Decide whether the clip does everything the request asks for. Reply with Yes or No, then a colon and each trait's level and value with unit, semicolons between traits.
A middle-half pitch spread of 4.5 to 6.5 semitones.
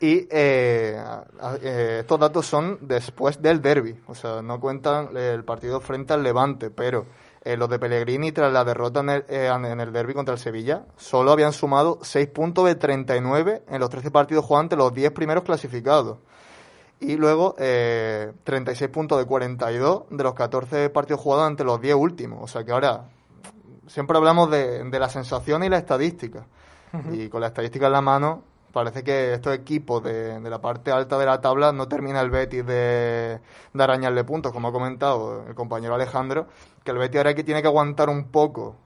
No: average, 3.5 semitones